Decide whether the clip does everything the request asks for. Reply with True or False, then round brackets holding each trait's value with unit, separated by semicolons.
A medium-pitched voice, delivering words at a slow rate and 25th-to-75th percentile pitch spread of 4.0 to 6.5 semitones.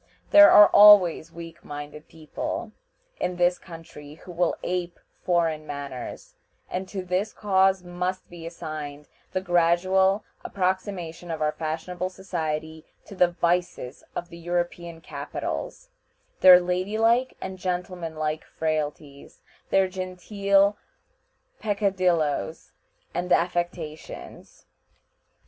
False (175 Hz; 105 wpm; 2.7 semitones)